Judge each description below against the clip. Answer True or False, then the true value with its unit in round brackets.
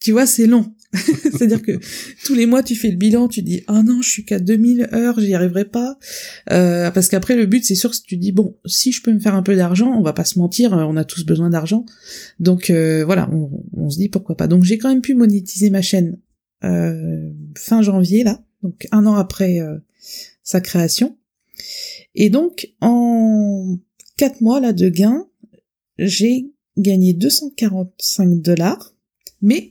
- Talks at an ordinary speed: True (195 wpm)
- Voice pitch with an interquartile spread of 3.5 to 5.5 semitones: True (4.3 semitones)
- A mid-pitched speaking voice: False (210 Hz)